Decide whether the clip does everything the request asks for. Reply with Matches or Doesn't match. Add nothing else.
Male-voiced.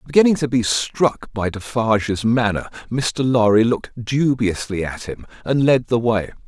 Matches